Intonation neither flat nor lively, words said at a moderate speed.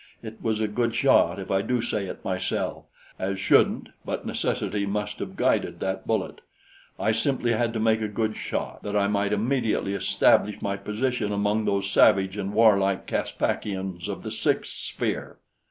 No: narrow, 2.1 semitones; average, 170 wpm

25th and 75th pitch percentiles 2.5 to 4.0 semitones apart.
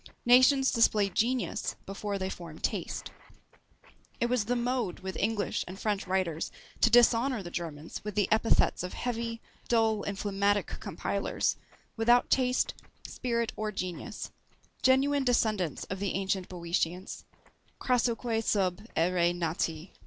No: average, 4.4 semitones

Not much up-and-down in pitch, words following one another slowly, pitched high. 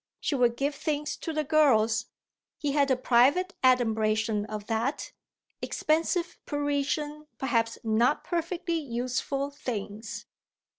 No: average, 4.8 semitones; slow, 115 wpm; very high, 270 Hz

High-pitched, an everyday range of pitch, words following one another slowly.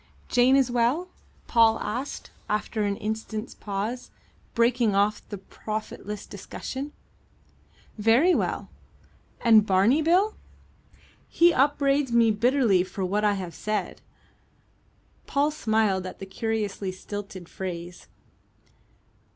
Yes: high, 220 Hz; average, 4.1 semitones; slow, 110 wpm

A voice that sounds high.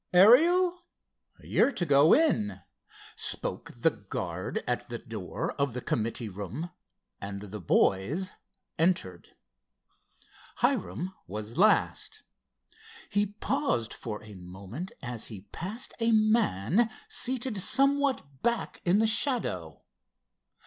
No: medium, 170 Hz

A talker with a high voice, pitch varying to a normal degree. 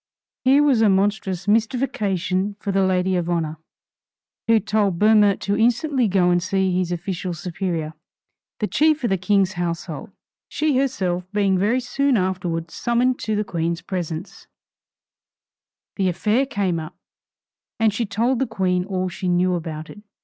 Yes: high, 195 Hz; average, 3.7 semitones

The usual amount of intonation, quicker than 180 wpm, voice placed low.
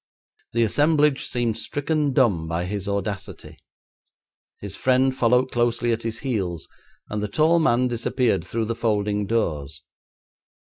No: average, 4.2 semitones; slow, 135 wpm; low, 115 Hz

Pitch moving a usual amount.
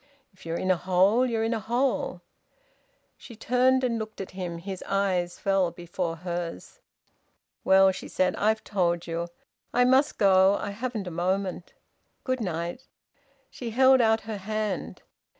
Yes: average, 4.1 semitones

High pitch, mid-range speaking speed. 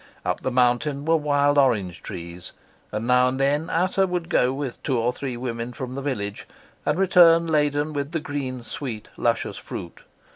No: low, 135 Hz; average, 180 wpm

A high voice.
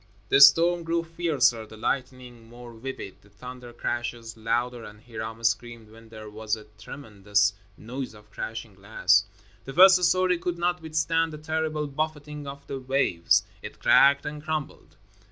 No: low, 125 Hz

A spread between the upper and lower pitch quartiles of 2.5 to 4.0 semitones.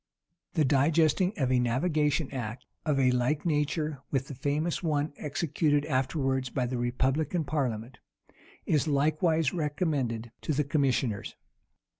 Yes: average, 3.1 semitones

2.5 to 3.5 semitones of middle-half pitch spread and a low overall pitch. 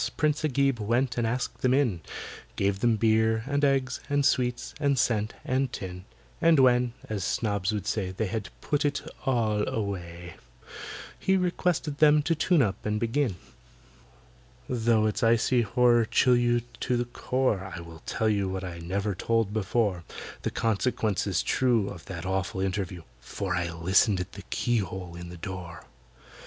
No: average, 5.0 semitones; low, 110 Hz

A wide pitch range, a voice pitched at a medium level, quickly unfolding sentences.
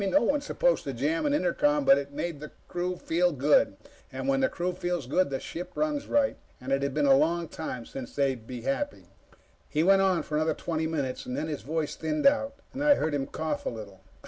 Yes: wide, 5.8 semitones; medium, 160 Hz; fast, 225 wpm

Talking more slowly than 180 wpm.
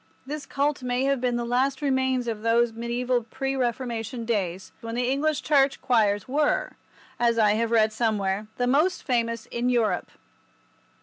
Yes: average, 165 wpm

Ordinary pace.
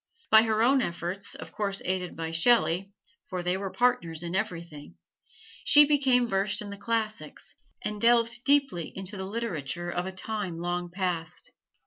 Yes: average, 160 wpm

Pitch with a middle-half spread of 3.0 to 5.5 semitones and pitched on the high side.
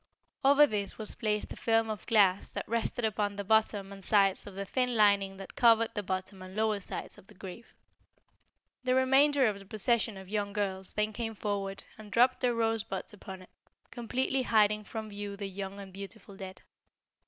No: narrow, 2.4 semitones; high, 210 Hz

